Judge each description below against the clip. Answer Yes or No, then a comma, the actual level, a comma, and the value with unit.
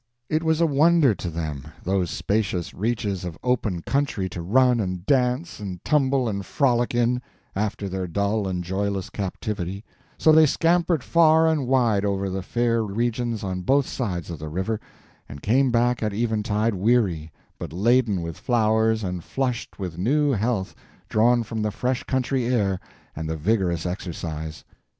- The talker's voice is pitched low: Yes, low, 110 Hz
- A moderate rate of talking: Yes, average, 160 wpm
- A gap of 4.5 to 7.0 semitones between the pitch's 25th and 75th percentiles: Yes, average, 5.1 semitones